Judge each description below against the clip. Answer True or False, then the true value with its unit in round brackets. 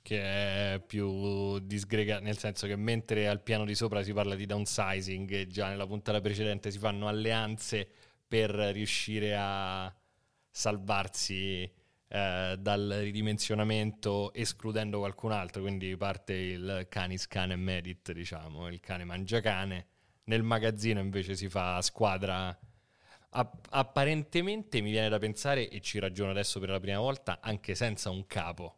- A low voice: True (100 Hz)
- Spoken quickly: False (145 wpm)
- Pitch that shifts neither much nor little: False (2.0 semitones)